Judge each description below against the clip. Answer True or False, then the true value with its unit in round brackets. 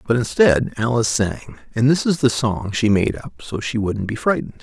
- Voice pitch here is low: True (115 Hz)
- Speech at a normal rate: False (220 wpm)